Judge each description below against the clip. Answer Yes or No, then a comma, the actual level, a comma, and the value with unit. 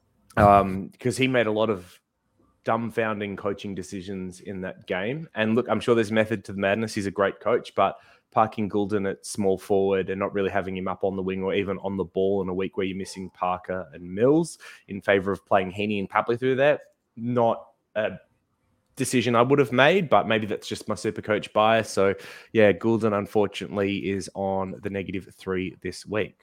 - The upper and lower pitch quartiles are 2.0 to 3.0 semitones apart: Yes, narrow, 2.5 semitones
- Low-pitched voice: Yes, low, 100 Hz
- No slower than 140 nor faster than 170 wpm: No, fast, 205 wpm